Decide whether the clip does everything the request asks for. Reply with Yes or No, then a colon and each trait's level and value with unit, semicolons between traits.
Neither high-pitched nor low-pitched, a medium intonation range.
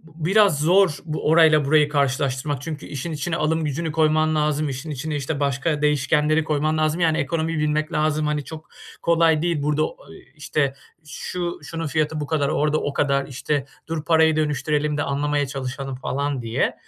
No: medium, 150 Hz; narrow, 1.9 semitones